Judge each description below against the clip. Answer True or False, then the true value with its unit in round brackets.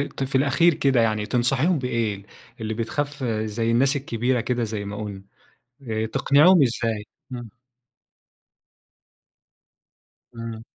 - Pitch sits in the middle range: False (120 Hz)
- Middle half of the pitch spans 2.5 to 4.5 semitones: True (3.6 semitones)